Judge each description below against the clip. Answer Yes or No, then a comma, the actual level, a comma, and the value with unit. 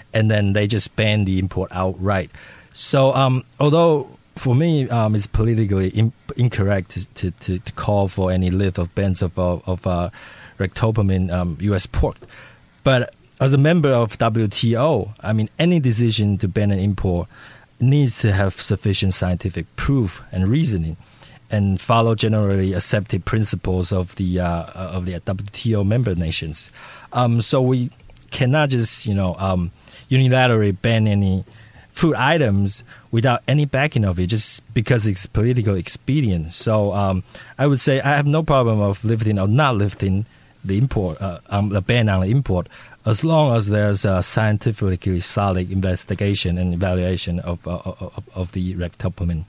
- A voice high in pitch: No, low, 105 Hz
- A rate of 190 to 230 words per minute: No, average, 160 wpm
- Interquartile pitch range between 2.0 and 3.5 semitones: No, average, 4.6 semitones